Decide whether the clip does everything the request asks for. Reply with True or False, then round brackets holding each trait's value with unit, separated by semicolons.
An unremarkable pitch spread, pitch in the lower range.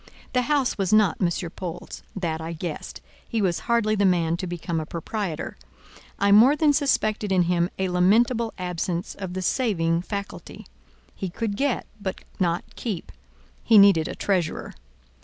False (4.0 semitones; 190 Hz)